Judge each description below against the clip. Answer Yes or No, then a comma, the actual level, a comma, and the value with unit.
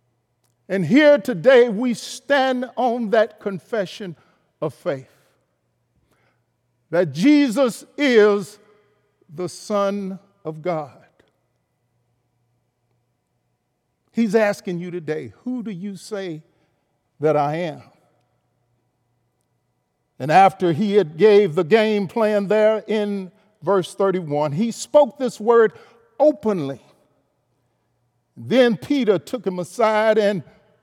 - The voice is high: Yes, high, 195 Hz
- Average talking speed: No, slow, 100 wpm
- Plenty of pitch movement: Yes, wide, 7.1 semitones